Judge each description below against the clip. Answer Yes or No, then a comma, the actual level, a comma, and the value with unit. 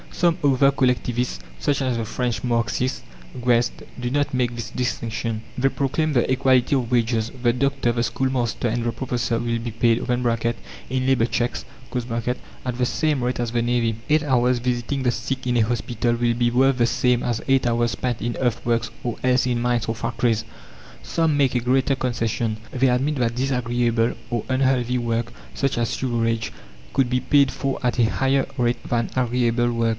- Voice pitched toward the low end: Yes, low, 120 Hz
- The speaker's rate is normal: Yes, average, 180 wpm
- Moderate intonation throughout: No, narrow, 1.7 semitones